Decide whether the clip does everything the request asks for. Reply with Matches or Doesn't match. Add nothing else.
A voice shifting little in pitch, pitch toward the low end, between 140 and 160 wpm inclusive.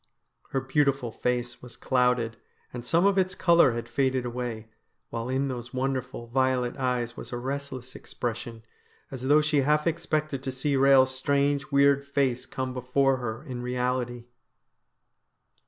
Matches